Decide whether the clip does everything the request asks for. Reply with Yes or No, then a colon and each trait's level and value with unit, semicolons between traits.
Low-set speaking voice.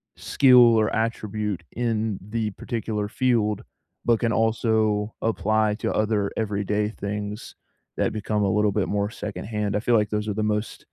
Yes: low, 105 Hz